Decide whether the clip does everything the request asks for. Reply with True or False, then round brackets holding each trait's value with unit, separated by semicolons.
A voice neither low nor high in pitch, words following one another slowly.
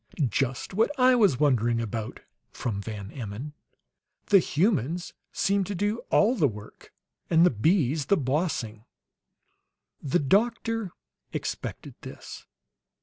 True (150 Hz; 120 wpm)